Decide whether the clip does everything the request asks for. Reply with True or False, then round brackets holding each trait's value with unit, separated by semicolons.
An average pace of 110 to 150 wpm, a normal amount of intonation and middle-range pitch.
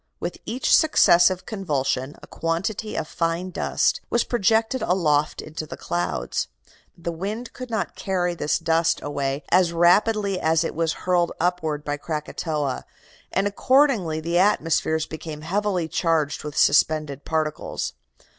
True (135 wpm; 3.9 semitones; 165 Hz)